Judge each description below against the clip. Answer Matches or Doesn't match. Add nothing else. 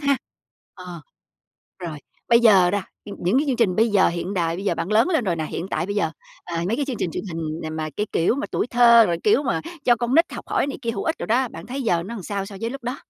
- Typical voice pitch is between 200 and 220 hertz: Matches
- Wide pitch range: Matches